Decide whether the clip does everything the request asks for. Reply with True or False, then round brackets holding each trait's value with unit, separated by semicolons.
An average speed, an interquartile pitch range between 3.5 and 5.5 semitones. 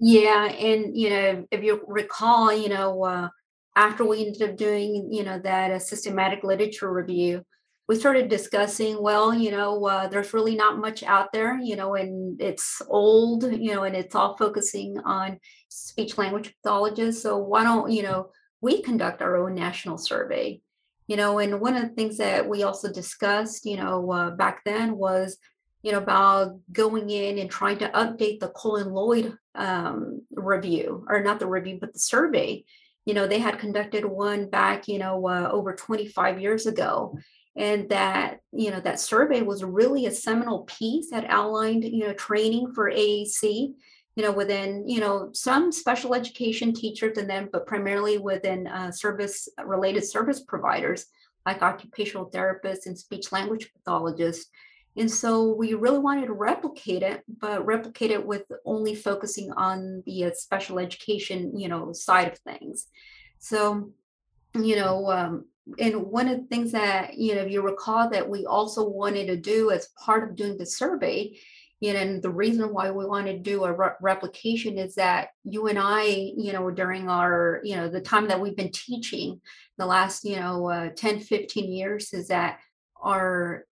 False (180 wpm; 2.4 semitones)